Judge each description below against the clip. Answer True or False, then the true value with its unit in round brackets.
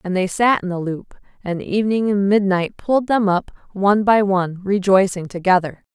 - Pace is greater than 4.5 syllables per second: True (5.3 syllables/s)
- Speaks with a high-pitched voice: True (195 Hz)